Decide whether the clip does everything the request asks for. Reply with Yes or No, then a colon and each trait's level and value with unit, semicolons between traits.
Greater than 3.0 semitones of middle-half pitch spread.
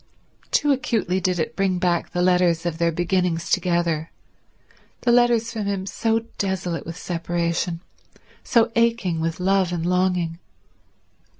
No: average, 2.7 semitones